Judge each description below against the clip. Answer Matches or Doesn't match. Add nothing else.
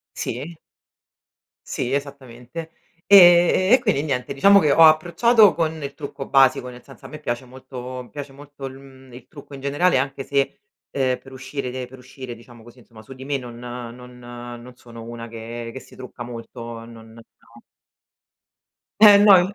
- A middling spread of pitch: Matches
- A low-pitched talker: Matches